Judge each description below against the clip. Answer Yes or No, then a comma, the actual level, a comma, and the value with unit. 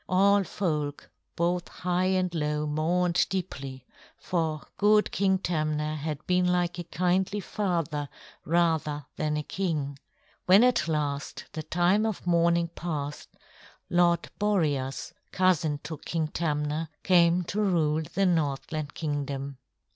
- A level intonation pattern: No, average, 3.2 semitones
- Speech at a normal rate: No, slow, 125 wpm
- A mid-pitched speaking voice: Yes, medium, 170 Hz